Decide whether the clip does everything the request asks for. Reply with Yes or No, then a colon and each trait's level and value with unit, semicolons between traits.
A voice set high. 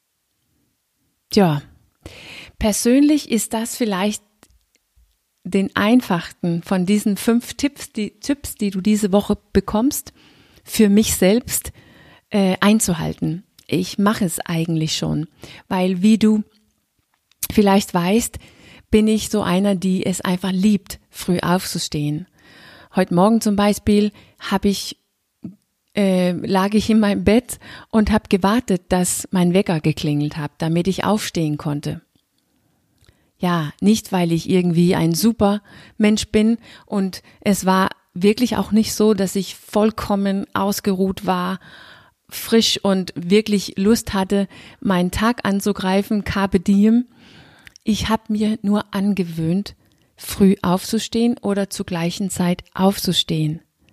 Yes: high, 200 Hz